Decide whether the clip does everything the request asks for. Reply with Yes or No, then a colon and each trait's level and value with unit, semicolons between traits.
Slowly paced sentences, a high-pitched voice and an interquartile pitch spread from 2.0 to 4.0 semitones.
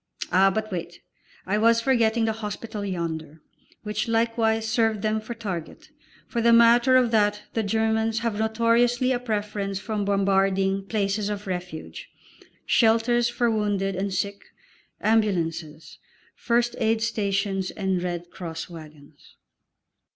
Yes: slow, 130 wpm; high, 210 Hz; average, 2.8 semitones